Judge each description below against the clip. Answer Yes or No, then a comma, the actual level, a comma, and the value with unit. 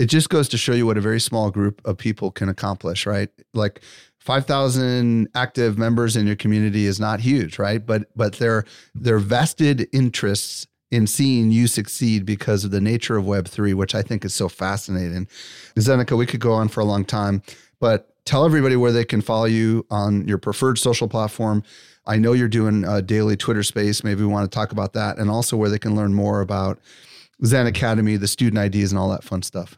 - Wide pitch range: No, narrow, 2.5 semitones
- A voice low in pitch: Yes, low, 110 Hz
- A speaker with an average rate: No, fast, 210 wpm